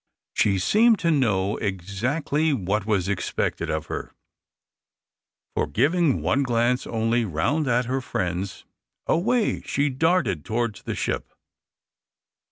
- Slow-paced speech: Yes, slow, 120 wpm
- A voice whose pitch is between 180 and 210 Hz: No, low, 120 Hz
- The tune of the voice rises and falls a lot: Yes, wide, 6.7 semitones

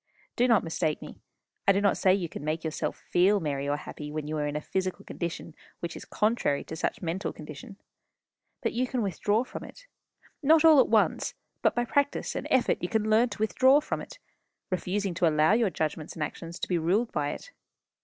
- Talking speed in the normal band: No, fast, 215 wpm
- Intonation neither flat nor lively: No, wide, 6.4 semitones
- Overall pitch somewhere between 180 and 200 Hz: Yes, medium, 185 Hz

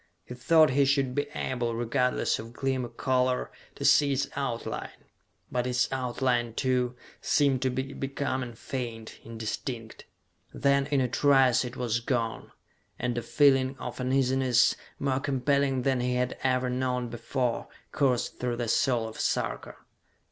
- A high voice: No, low, 125 Hz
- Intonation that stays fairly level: Yes, narrow, 1.8 semitones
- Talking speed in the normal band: Yes, average, 150 wpm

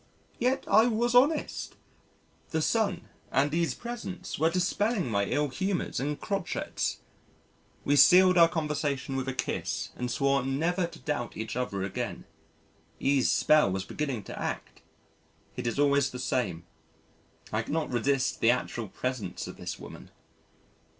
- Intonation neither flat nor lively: No, wide, 6.1 semitones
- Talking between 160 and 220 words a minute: No, average, 145 wpm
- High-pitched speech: No, medium, 145 Hz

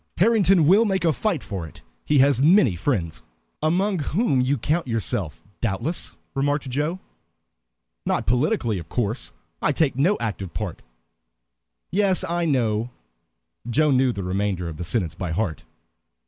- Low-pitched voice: Yes, low, 130 Hz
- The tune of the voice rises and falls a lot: Yes, wide, 8.7 semitones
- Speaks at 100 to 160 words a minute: Yes, average, 145 wpm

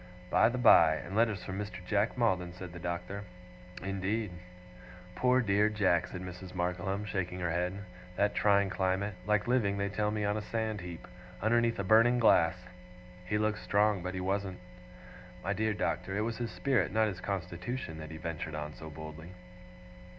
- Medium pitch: No, low, 100 Hz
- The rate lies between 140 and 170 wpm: No, average, 180 wpm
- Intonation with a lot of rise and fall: No, average, 3.0 semitones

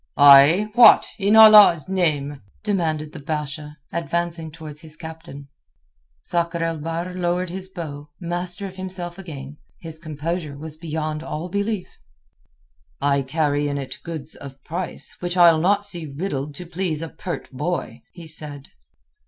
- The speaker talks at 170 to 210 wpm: No, average, 145 wpm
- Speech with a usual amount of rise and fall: Yes, average, 3.1 semitones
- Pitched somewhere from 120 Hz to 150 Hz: No, medium, 165 Hz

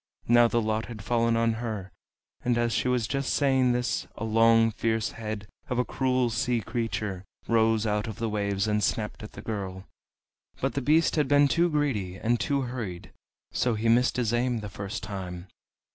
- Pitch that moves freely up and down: No, average, 2.7 semitones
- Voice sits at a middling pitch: No, low, 115 Hz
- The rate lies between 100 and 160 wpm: No, average, 190 wpm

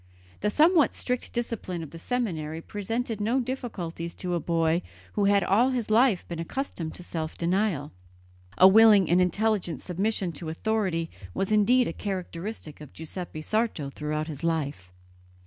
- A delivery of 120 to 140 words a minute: No, average, 155 wpm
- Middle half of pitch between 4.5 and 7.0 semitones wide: Yes, average, 5.2 semitones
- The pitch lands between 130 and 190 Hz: Yes, medium, 185 Hz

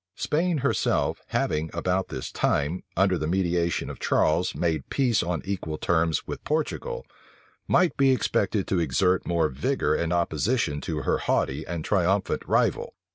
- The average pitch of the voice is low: Yes, very low, 90 Hz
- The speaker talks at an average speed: Yes, average, 150 wpm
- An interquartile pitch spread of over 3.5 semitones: Yes, average, 4.2 semitones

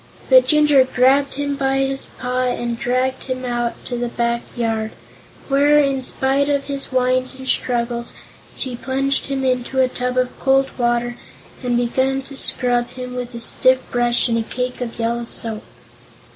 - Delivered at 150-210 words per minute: Yes, average, 170 wpm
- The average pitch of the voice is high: Yes, very high, 255 Hz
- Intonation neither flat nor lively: No, narrow, 2.0 semitones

